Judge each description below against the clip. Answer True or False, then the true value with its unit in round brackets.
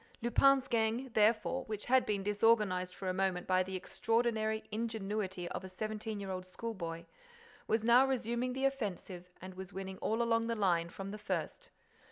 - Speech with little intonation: False (3.6 semitones)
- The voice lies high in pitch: True (215 Hz)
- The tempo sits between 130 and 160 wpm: False (175 wpm)